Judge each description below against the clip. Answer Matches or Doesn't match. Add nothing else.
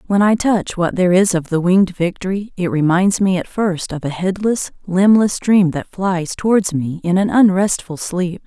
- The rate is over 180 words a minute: Matches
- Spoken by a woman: Matches